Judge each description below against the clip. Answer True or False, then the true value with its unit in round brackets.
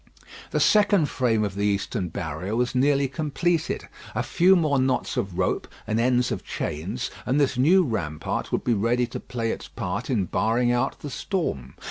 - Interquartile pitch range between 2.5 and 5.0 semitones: False (5.6 semitones)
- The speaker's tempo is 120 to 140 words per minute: False (180 wpm)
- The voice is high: False (125 Hz)